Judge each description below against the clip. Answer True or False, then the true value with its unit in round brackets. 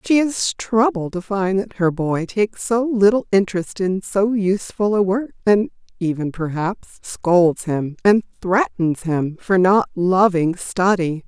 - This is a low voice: False (195 Hz)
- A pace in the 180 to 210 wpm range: False (155 wpm)